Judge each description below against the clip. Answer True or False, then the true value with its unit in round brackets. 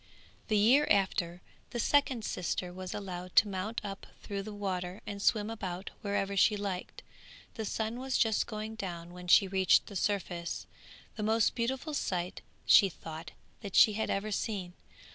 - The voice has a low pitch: False (200 Hz)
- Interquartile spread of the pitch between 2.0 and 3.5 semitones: True (3.2 semitones)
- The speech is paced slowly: False (165 wpm)